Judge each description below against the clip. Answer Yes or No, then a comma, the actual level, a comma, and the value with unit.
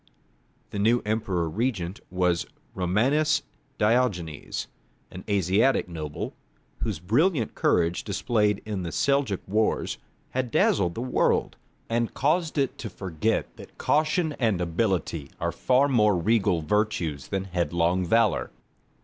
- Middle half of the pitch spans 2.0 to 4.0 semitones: No, wide, 5.4 semitones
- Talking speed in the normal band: No, slow, 125 wpm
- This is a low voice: Yes, low, 105 Hz